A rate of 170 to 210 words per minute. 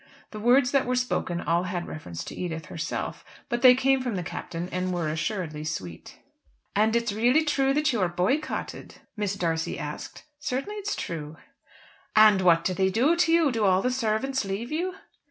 Yes: average, 190 wpm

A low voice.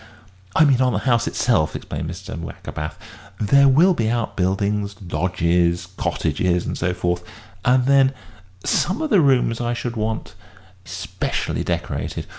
Yes: low, 110 Hz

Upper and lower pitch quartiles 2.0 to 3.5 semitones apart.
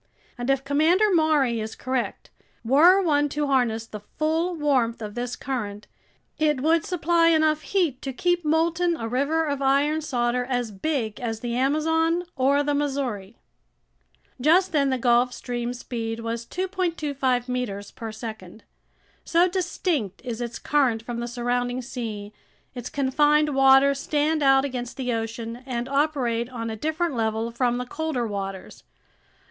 No: average, 4.5 semitones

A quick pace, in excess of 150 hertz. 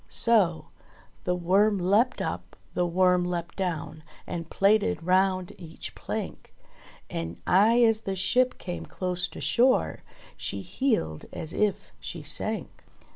No: slow, 135 wpm; medium, 185 Hz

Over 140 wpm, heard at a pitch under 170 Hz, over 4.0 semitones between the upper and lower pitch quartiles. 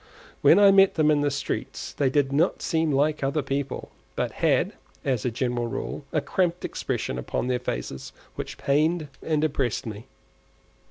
No: average, 170 wpm; medium, 140 Hz; average, 3.5 semitones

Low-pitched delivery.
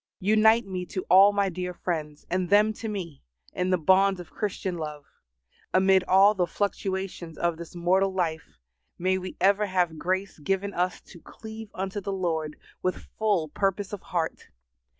No: medium, 185 Hz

